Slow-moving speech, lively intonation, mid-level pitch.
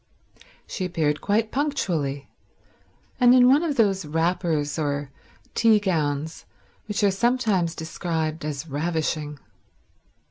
Yes: slow, 110 wpm; wide, 5.8 semitones; medium, 170 Hz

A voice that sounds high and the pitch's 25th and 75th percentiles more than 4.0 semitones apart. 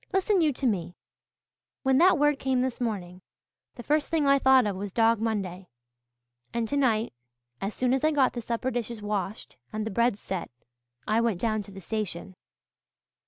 Yes: high, 230 Hz; average, 4.4 semitones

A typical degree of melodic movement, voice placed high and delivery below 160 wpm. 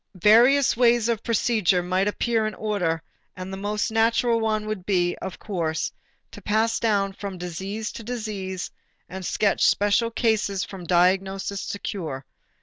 Yes: average, 3.0 semitones; high, 205 Hz; average, 150 wpm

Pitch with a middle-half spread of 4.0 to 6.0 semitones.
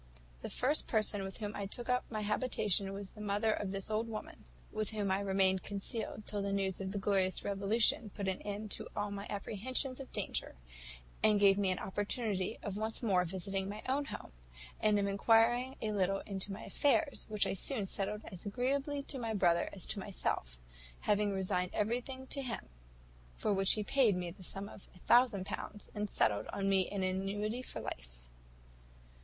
No: narrow, 2.4 semitones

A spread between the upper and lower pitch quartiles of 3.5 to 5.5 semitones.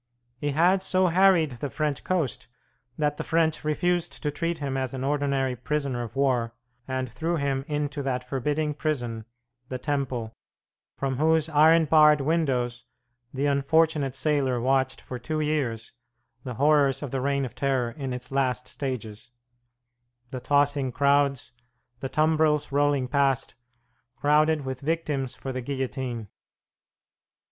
No: average, 2.8 semitones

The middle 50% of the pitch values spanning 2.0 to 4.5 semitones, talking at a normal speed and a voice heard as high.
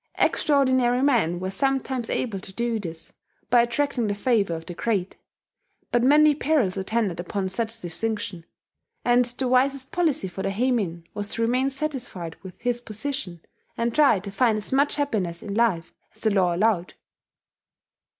No: average, 5.2 semitones; average, 160 wpm; high, 225 Hz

